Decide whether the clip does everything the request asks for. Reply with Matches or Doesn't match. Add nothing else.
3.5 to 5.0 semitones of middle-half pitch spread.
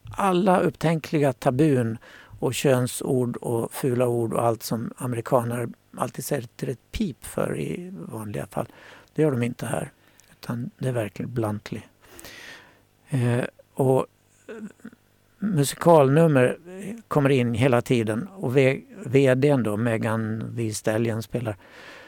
Matches